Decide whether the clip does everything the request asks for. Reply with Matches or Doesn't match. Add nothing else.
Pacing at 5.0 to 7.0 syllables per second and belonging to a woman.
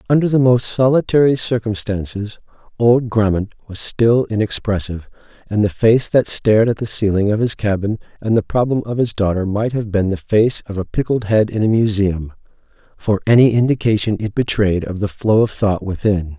Doesn't match